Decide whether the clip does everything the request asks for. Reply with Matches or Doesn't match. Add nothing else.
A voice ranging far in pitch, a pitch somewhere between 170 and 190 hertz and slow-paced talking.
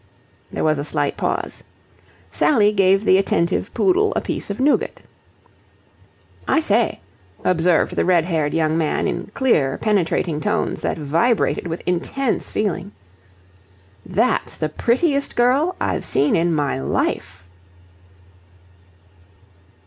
Matches